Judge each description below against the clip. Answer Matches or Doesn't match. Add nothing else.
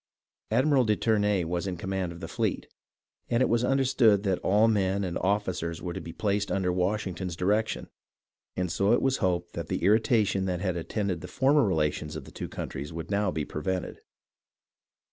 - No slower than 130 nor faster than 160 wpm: Doesn't match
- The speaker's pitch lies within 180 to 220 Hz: Doesn't match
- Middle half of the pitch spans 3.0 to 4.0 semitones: Matches